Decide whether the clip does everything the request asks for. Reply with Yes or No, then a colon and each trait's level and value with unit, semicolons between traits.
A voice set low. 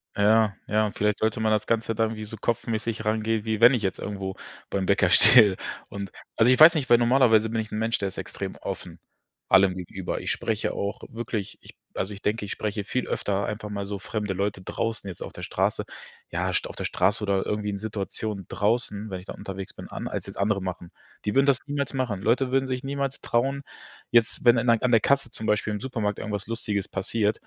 Yes: low, 110 Hz